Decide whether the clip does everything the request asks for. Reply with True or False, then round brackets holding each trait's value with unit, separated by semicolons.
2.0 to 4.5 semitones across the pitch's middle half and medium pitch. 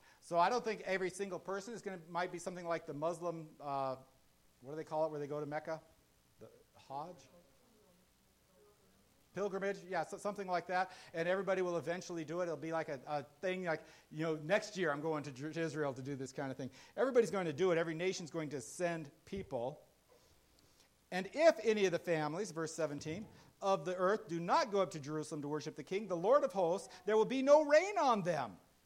True (3.9 semitones; 170 Hz)